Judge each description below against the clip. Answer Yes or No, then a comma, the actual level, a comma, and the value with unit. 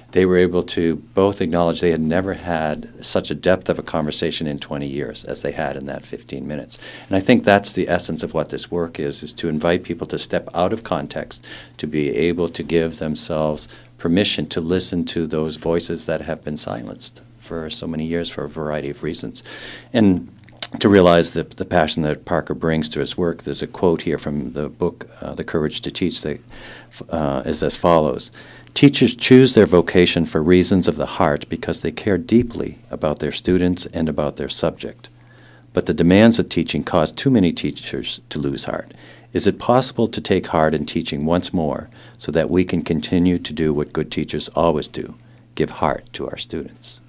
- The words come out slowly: No, fast, 205 wpm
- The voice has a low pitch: Yes, very low, 85 Hz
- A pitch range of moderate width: Yes, average, 3.0 semitones